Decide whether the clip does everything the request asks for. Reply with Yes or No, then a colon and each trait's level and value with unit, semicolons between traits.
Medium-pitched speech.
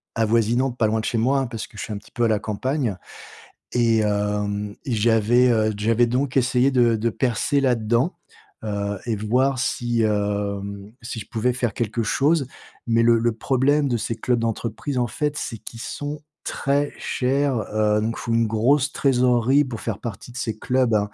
No: low, 115 Hz